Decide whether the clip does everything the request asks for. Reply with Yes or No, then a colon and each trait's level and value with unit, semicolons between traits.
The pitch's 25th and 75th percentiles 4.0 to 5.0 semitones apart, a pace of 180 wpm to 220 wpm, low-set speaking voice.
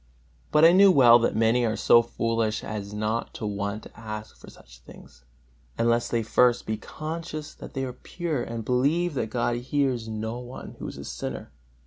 No: average, 3.5 semitones; average, 190 wpm; low, 120 Hz